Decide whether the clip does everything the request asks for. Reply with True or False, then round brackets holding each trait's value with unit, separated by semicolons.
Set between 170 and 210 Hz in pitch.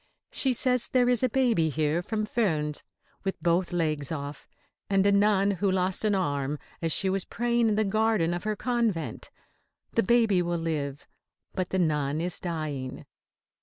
True (185 Hz)